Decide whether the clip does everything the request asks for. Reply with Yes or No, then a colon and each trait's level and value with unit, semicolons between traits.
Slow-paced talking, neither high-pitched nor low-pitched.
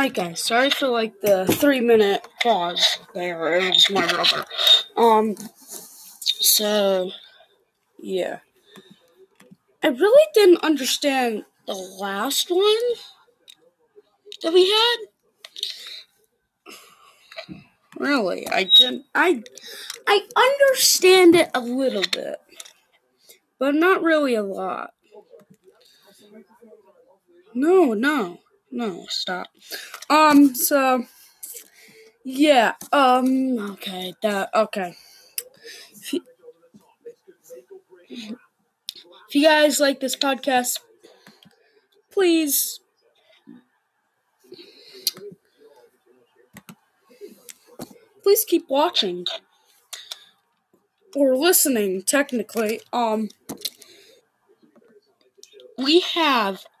No: slow, 75 wpm; very high, 295 Hz